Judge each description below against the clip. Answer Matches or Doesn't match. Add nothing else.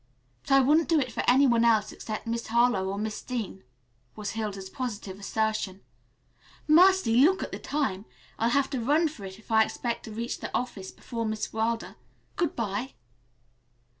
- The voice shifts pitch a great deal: Doesn't match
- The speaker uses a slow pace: Doesn't match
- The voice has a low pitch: Doesn't match